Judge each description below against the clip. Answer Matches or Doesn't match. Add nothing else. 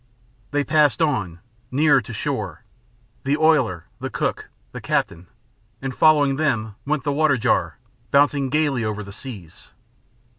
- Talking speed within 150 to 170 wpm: Doesn't match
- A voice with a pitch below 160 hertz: Matches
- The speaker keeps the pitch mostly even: Doesn't match